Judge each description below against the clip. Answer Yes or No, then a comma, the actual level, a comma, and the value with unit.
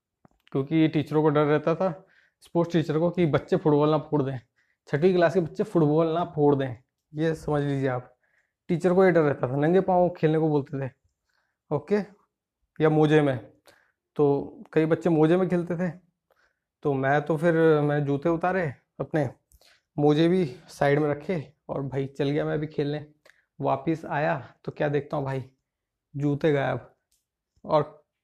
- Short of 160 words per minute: No, average, 170 wpm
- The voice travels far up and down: No, average, 2.9 semitones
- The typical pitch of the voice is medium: Yes, medium, 155 Hz